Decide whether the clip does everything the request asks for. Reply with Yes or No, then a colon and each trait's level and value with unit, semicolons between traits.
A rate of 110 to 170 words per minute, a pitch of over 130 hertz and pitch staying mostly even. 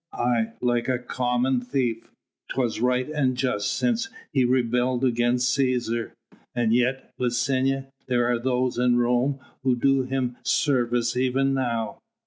No: slow, 135 wpm; low, 125 Hz; narrow, 1.5 semitones